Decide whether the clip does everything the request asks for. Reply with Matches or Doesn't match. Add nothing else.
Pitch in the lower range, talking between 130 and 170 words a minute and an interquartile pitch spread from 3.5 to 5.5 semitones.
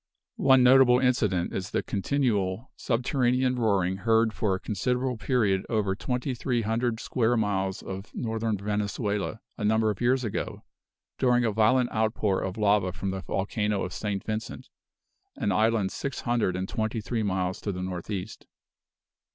Matches